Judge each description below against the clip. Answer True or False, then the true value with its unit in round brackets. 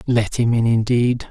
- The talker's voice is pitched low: True (115 Hz)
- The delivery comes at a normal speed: True (185 wpm)